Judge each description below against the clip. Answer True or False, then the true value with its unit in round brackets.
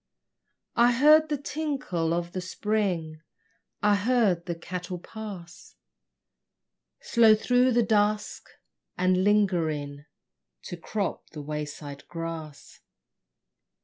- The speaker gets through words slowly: True (100 wpm)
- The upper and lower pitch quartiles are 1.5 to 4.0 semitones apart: False (4.8 semitones)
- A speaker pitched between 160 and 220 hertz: True (185 Hz)